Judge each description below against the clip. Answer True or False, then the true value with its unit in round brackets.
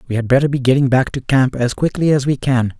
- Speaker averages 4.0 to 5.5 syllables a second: False (6.1 syllables/s)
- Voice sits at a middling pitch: False (130 Hz)